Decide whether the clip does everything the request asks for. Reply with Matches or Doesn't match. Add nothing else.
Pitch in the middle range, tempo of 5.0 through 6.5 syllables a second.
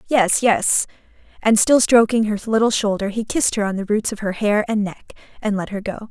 Doesn't match